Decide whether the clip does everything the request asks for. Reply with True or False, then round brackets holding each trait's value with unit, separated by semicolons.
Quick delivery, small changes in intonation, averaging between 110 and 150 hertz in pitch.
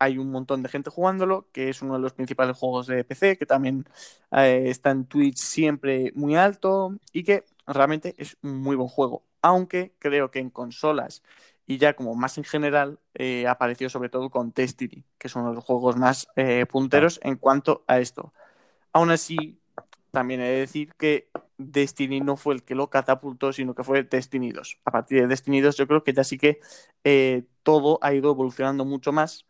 True (200 wpm; 2.3 semitones; 135 Hz)